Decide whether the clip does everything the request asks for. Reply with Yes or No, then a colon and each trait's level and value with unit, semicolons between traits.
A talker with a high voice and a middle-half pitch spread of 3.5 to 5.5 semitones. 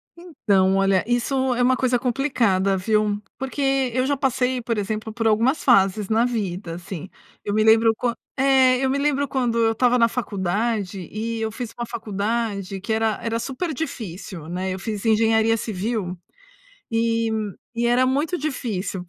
Yes: high, 225 Hz; average, 3.8 semitones